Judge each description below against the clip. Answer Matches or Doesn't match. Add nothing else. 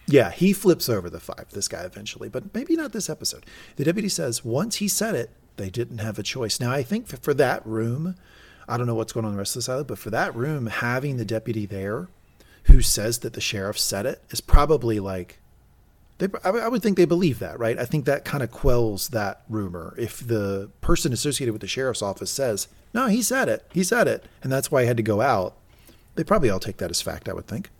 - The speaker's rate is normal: Doesn't match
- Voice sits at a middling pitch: Doesn't match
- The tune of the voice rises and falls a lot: Matches